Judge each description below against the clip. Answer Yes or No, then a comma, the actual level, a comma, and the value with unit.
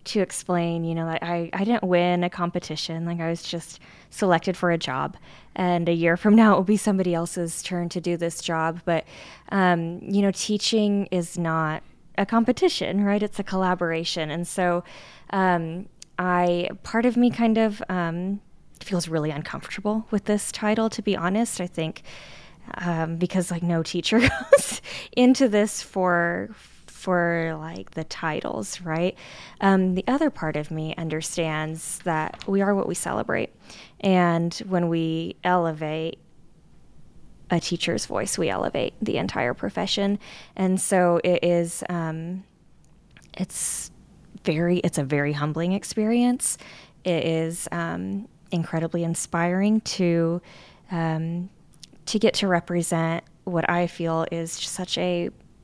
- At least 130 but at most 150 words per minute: Yes, average, 145 wpm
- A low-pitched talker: No, medium, 175 Hz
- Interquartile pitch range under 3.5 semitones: Yes, average, 2.7 semitones